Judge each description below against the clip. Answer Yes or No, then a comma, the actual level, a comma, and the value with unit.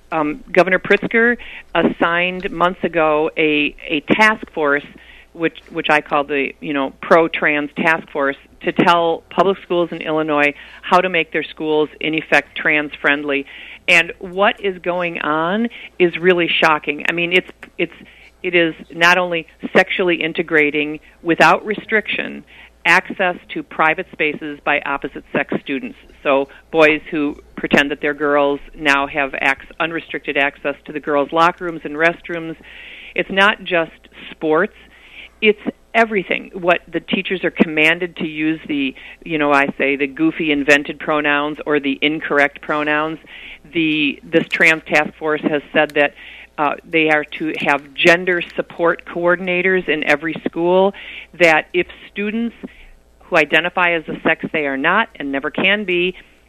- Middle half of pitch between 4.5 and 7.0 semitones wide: No, average, 3.5 semitones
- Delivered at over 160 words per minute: No, average, 150 wpm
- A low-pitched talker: No, medium, 160 Hz